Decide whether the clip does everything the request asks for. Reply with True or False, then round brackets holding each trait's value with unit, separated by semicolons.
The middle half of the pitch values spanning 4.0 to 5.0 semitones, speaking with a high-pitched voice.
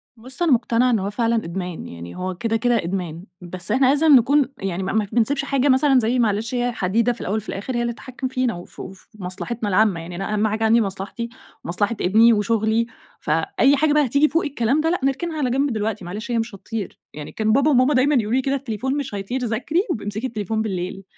True (4.5 semitones; 225 Hz)